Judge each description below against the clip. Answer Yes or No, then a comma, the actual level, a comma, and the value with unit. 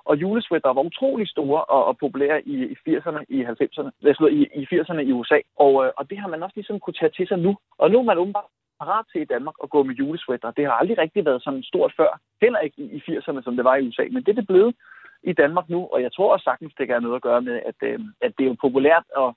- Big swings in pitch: Yes, wide, 7.1 semitones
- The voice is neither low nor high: Yes, medium, 155 Hz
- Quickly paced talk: Yes, fast, 265 wpm